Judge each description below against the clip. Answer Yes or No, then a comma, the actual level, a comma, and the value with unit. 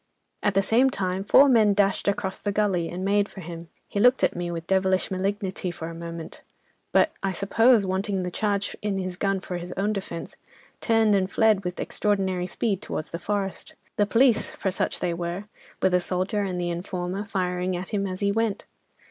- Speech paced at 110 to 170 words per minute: No, average, 195 wpm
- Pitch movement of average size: No, narrow, 2.3 semitones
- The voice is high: Yes, high, 195 Hz